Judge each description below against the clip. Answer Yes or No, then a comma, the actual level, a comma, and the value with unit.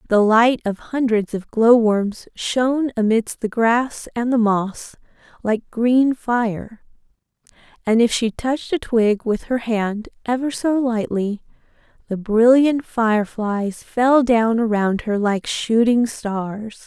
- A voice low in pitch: No, high, 230 Hz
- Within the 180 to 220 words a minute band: No, slow, 135 wpm